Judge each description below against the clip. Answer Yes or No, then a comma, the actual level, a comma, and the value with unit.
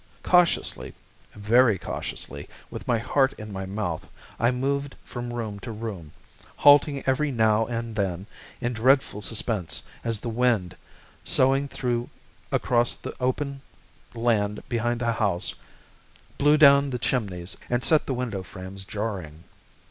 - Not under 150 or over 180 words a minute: No, slow, 135 wpm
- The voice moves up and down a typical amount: Yes, average, 4.1 semitones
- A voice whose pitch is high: No, low, 115 Hz